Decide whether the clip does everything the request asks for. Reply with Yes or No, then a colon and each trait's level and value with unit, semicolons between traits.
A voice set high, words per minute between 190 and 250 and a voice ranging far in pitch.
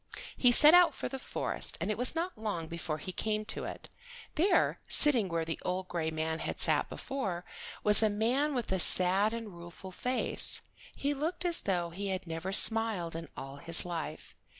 Yes: high, 195 Hz; average, 195 wpm; wide, 6.6 semitones